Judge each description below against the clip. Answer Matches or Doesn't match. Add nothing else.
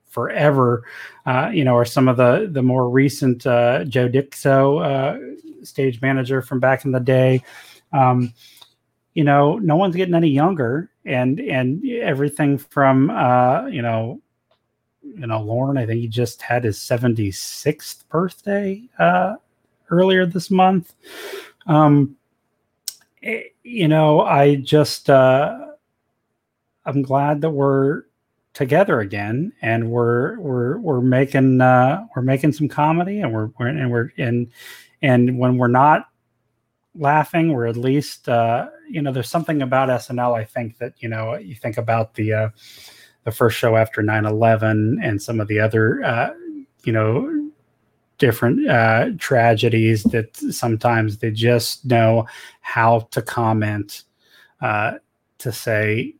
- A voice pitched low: Matches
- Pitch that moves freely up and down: Doesn't match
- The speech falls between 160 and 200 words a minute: Doesn't match